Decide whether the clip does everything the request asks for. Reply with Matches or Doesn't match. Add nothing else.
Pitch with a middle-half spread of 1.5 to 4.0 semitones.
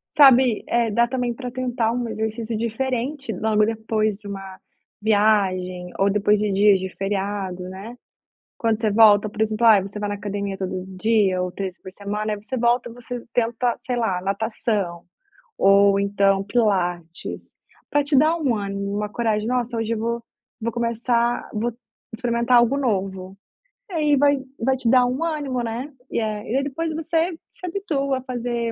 Matches